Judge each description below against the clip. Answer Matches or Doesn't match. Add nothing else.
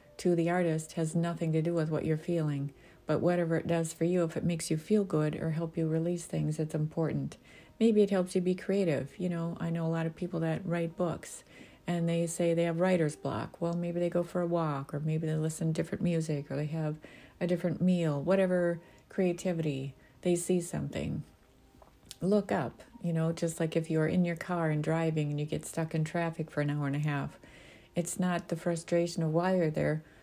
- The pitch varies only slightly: Matches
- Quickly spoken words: Matches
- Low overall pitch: Doesn't match